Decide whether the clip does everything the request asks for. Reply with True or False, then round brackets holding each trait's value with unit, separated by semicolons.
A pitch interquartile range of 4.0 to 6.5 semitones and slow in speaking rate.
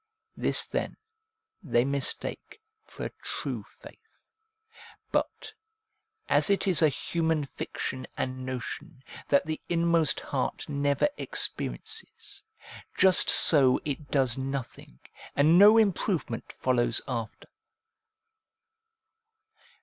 True (4.7 semitones; 100 wpm)